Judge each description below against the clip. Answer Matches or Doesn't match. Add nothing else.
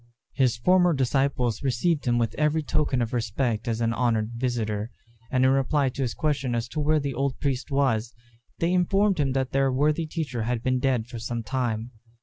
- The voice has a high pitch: Doesn't match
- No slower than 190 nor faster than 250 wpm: Matches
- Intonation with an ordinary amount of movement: Matches